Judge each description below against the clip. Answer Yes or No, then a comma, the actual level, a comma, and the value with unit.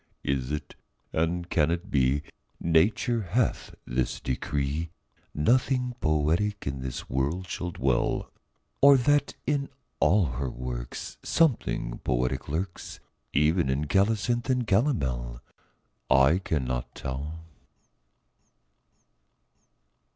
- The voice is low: Yes, very low, 80 Hz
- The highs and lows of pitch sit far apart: Yes, wide, 7.8 semitones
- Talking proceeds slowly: Yes, slow, 100 wpm